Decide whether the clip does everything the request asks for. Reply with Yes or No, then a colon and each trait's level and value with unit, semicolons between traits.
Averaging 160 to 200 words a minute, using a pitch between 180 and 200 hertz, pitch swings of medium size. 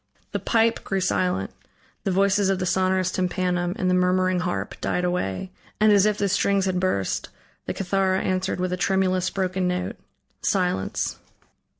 No: average, 165 wpm; medium, 185 Hz; narrow, 1.1 semitones